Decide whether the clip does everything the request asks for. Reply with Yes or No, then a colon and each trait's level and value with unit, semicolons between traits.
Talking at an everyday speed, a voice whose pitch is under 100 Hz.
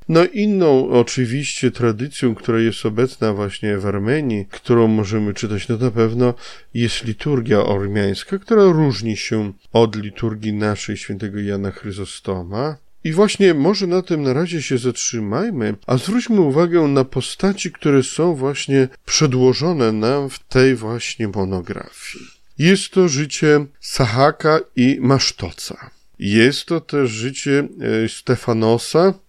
No: average, 125 wpm; low, 125 Hz